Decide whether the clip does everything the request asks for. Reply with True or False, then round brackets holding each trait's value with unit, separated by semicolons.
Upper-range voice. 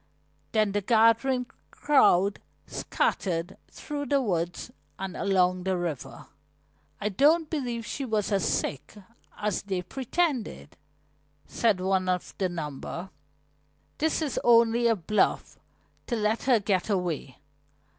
True (205 Hz)